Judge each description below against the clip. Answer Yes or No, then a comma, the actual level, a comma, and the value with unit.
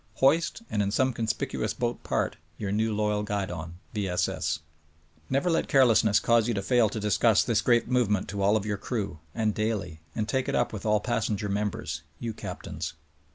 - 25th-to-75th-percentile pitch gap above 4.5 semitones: No, narrow, 2.6 semitones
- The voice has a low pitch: Yes, low, 105 Hz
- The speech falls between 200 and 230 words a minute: Yes, fast, 205 wpm